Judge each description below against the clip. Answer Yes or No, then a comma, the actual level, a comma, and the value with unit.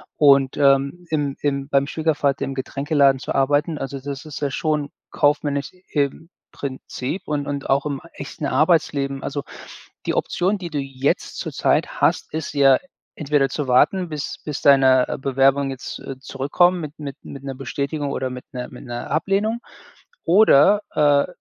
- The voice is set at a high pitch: No, medium, 140 Hz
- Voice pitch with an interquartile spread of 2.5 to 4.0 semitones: No, narrow, 1.9 semitones